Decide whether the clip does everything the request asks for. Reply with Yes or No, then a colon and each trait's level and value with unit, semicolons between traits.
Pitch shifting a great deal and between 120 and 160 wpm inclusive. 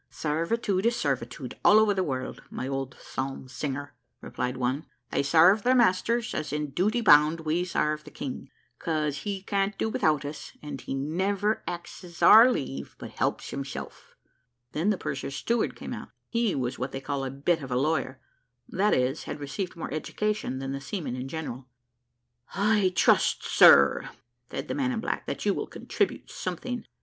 No: wide, 6.9 semitones; average, 180 wpm